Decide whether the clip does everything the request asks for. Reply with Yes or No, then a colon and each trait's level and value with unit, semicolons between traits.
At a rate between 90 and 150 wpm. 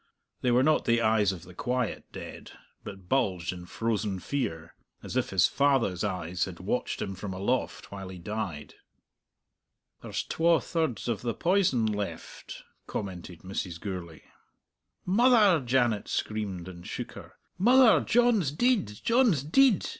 Yes: average, 145 wpm